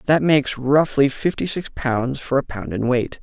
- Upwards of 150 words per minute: Yes, fast, 205 wpm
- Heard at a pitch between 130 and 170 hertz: Yes, low, 135 Hz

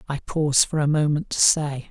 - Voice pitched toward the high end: No, medium, 145 Hz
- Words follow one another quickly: Yes, fast, 220 wpm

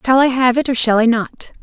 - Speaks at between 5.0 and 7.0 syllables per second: Yes, 5.6 syllables/s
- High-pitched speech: Yes, high, 245 Hz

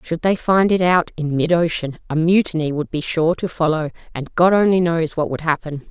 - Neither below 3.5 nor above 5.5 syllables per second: Yes, 5.2 syllables/s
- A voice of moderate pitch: Yes, medium, 165 Hz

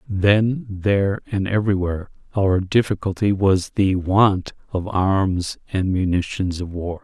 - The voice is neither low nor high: No, very low, 95 Hz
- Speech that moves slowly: Yes, slow, 130 wpm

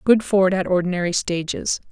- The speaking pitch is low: No, medium, 185 Hz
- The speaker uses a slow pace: No, average, 155 wpm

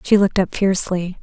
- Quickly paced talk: No, average, 195 wpm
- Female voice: Yes, female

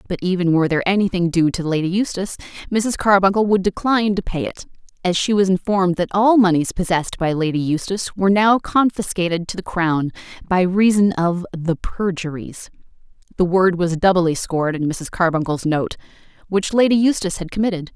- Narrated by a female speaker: Yes, female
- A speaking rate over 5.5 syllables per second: Yes, 5.8 syllables/s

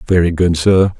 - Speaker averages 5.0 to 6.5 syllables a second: Yes, 5.1 syllables/s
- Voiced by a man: Yes, male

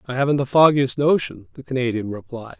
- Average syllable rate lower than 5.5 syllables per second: No, 5.9 syllables/s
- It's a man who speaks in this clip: Yes, male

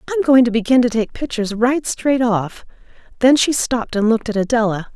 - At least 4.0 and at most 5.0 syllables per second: No, 5.8 syllables/s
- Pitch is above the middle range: Yes, high, 240 Hz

